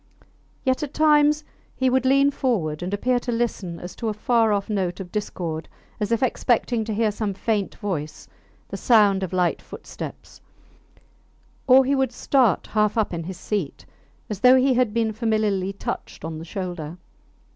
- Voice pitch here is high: Yes, high, 215 Hz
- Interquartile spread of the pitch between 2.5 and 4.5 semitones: No, average, 5.1 semitones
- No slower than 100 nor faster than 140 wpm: No, average, 175 wpm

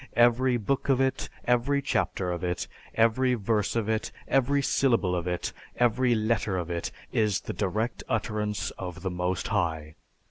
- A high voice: No, low, 110 Hz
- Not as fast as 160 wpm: No, average, 165 wpm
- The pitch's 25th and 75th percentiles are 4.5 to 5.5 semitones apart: Yes, average, 5.1 semitones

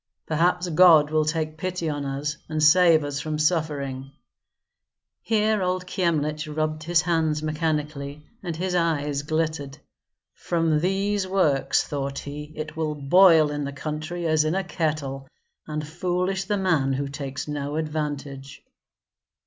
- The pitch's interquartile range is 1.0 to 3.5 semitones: Yes, average, 2.8 semitones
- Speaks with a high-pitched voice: No, medium, 155 Hz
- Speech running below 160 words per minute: Yes, average, 140 wpm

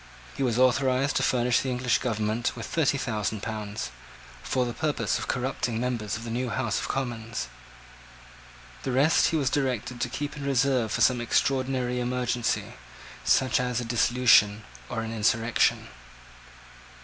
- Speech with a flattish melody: Yes, narrow, 2.3 semitones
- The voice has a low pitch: Yes, low, 125 Hz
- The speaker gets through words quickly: No, average, 155 wpm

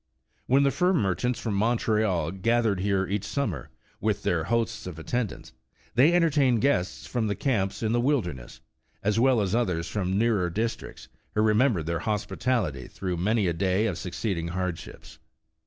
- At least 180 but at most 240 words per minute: No, average, 160 wpm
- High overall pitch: No, low, 105 Hz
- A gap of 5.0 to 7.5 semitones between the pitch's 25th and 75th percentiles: No, average, 4.5 semitones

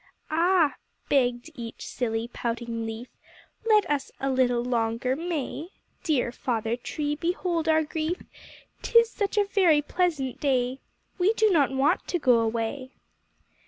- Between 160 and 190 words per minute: No, slow, 135 wpm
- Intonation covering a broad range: Yes, wide, 5.7 semitones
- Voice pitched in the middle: No, very high, 275 Hz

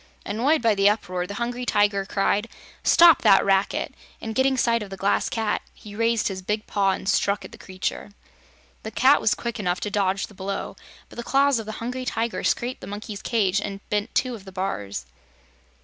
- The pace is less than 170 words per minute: No, fast, 205 wpm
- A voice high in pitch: Yes, high, 210 Hz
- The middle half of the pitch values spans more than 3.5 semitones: No, average, 3.0 semitones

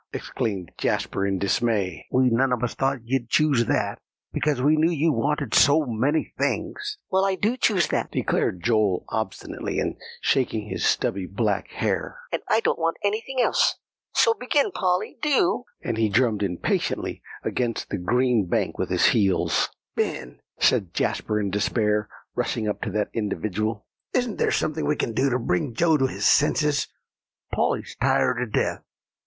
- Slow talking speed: No, average, 165 wpm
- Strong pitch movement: Yes, wide, 6.4 semitones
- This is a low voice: Yes, low, 120 Hz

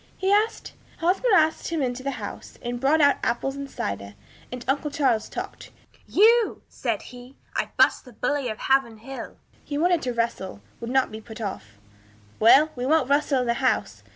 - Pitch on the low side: No, very high, 265 Hz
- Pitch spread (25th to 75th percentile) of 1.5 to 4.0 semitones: No, average, 4.4 semitones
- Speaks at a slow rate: No, average, 180 wpm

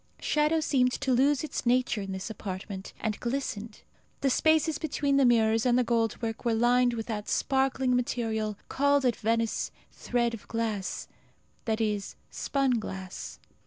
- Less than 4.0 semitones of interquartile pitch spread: Yes, average, 3.4 semitones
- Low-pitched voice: No, high, 235 Hz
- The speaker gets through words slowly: No, average, 160 wpm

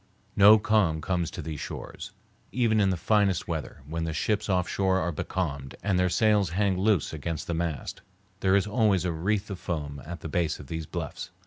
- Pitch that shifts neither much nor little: Yes, average, 3.9 semitones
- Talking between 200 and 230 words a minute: Yes, fast, 205 wpm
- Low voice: Yes, very low, 90 Hz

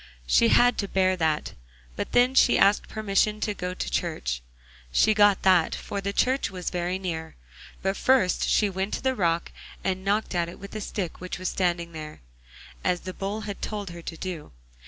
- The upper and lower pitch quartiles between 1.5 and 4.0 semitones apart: Yes, average, 3.1 semitones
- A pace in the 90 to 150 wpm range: No, average, 200 wpm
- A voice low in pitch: No, medium, 185 Hz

